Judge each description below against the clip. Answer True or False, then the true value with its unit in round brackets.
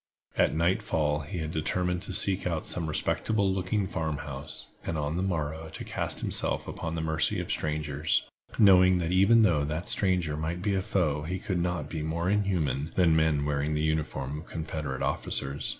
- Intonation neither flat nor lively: True (3.2 semitones)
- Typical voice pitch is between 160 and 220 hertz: False (80 Hz)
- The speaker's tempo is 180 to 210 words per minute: True (185 wpm)